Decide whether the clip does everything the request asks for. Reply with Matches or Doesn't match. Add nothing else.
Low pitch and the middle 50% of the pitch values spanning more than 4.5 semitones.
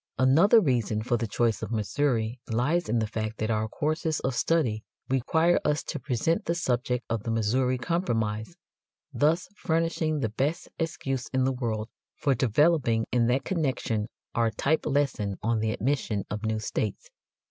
Matches